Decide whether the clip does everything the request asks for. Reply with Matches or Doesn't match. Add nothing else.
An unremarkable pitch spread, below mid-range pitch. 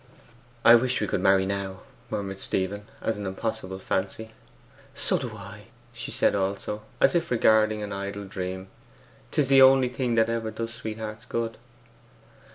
Matches